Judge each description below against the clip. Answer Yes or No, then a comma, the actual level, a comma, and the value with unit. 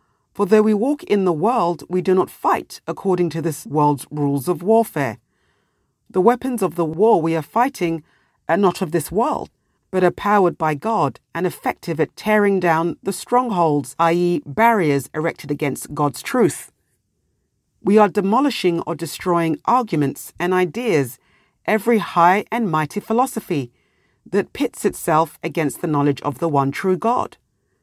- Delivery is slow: No, average, 155 wpm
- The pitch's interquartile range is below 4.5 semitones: No, average, 5.1 semitones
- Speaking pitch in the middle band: Yes, medium, 175 Hz